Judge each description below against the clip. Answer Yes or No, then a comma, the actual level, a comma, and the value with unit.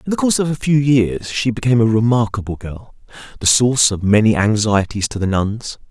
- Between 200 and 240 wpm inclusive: Yes, fast, 205 wpm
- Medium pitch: No, low, 115 Hz